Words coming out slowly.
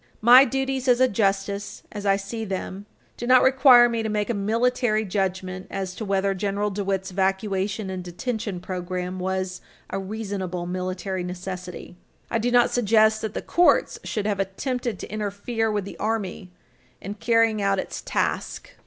No: average, 165 wpm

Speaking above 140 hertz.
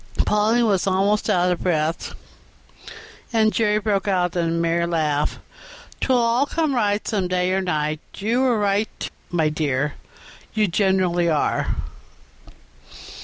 Yes: high, 190 Hz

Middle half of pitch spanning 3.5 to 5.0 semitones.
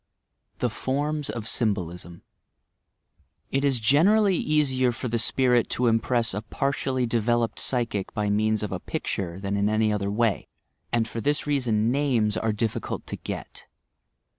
Yes: average, 3.9 semitones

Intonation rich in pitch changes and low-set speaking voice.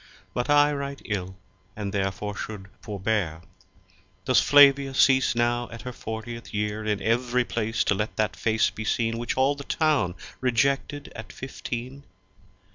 No: average, 4.0 semitones; low, 115 Hz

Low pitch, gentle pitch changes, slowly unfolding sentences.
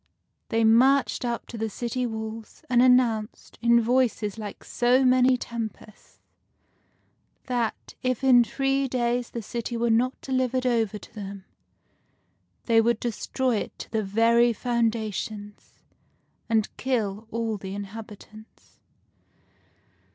No: high, 230 Hz; narrow, 2.3 semitones; slow, 125 wpm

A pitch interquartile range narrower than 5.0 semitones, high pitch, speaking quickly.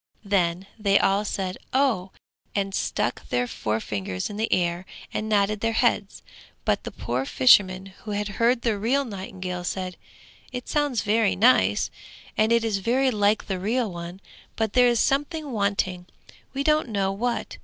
No: average, 4.0 semitones; high, 205 Hz; average, 165 wpm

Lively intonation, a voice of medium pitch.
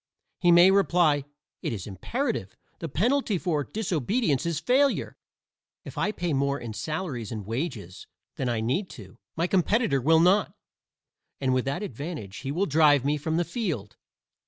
Yes: wide, 6.1 semitones; medium, 155 Hz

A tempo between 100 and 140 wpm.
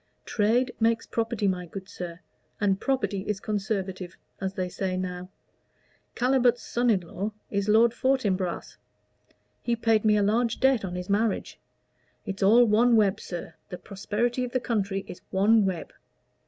No: average, 155 wpm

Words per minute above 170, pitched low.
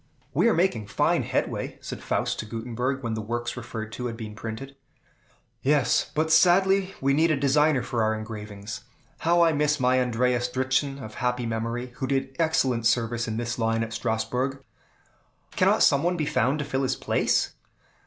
Yes: average, 180 wpm; low, 125 Hz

